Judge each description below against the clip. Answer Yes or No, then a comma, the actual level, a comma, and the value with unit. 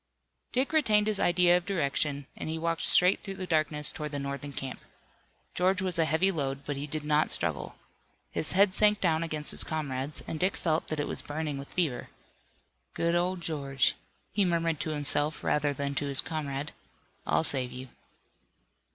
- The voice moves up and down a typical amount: Yes, average, 3.9 semitones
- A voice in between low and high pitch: Yes, medium, 155 Hz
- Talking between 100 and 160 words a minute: No, average, 185 wpm